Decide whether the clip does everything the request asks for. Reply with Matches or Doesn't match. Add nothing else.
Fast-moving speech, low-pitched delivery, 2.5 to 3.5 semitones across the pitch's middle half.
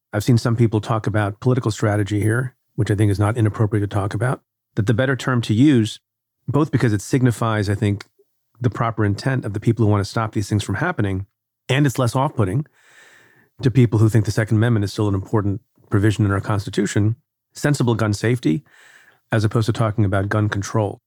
Matches